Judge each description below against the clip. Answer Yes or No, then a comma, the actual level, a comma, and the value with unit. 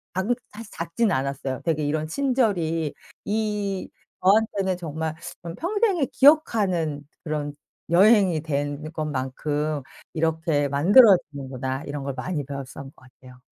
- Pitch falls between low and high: Yes, medium, 160 Hz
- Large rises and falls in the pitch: Yes, wide, 5.8 semitones